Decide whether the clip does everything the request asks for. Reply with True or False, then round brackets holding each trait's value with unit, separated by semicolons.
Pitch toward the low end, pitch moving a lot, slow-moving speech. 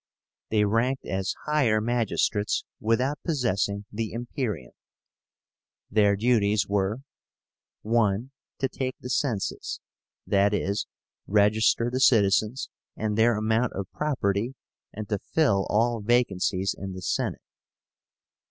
False (110 Hz; 3.3 semitones; 110 wpm)